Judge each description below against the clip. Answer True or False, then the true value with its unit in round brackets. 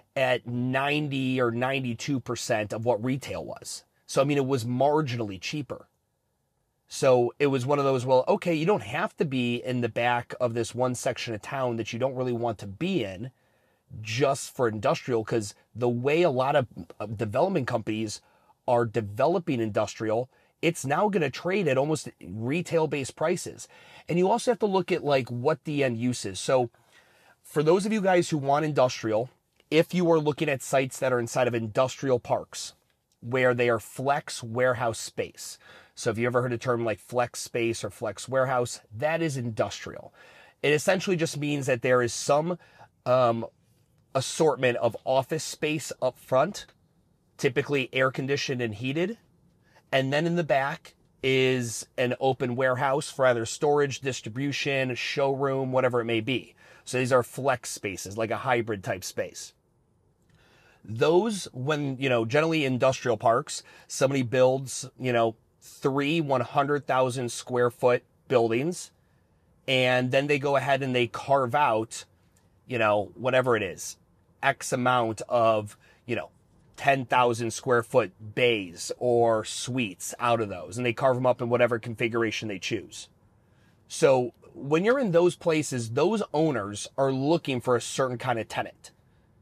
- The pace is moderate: True (160 wpm)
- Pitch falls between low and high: False (130 Hz)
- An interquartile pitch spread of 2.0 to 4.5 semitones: True (3.2 semitones)